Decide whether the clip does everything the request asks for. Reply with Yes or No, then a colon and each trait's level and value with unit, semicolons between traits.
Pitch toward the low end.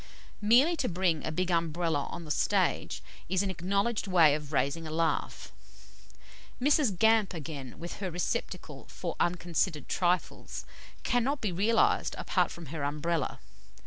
No: medium, 175 Hz